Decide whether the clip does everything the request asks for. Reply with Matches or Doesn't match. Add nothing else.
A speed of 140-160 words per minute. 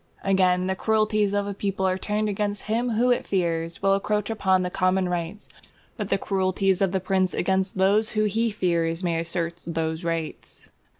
Doesn't match